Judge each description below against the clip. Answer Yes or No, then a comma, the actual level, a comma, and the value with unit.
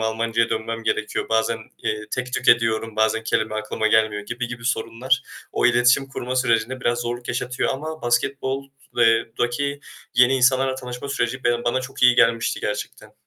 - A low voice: Yes, low, 120 Hz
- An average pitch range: No, narrow, 2.2 semitones